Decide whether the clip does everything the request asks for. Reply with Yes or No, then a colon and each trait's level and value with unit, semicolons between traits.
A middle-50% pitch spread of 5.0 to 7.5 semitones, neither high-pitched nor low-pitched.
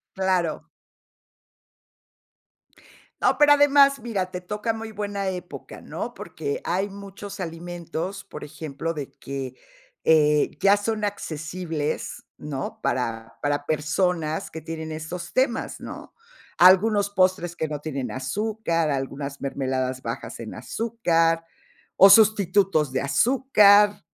Yes: average, 5.3 semitones; medium, 175 Hz